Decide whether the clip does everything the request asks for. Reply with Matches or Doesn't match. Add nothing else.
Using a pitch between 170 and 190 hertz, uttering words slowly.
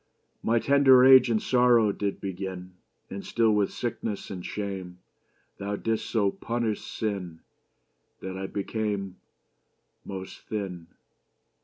Doesn't match